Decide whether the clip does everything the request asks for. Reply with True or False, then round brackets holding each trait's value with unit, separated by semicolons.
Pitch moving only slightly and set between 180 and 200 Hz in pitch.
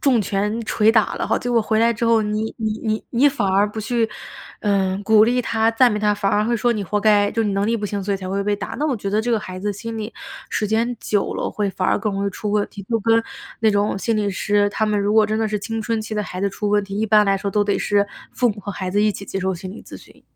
False (1.8 semitones; 210 Hz)